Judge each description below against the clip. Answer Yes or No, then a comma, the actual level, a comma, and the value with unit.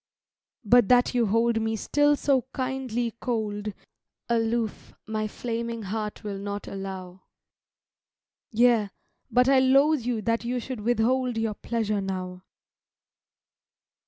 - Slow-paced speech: Yes, slow, 120 wpm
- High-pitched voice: Yes, high, 230 Hz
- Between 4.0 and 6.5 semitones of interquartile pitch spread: No, average, 2.8 semitones